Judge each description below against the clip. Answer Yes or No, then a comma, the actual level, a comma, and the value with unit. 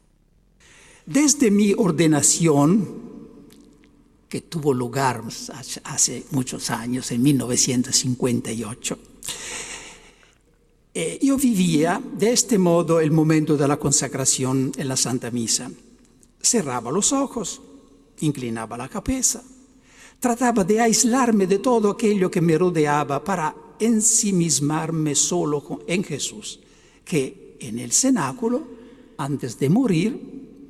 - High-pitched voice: No, medium, 170 Hz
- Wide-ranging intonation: Yes, wide, 8.7 semitones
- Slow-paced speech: Yes, slow, 105 wpm